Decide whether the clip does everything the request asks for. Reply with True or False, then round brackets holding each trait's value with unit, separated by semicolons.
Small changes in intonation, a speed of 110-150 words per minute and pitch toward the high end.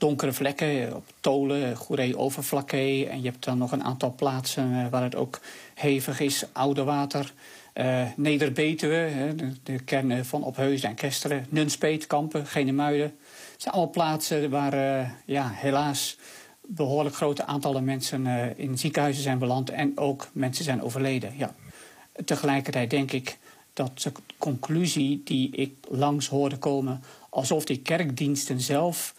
False (1.8 semitones; 145 wpm; 140 Hz)